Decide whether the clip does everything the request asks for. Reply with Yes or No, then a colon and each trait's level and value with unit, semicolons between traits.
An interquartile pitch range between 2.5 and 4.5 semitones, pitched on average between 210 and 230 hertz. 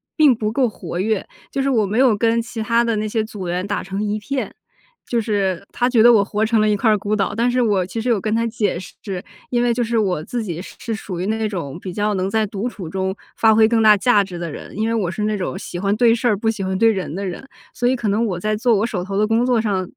Yes: average, 3.0 semitones; high, 215 Hz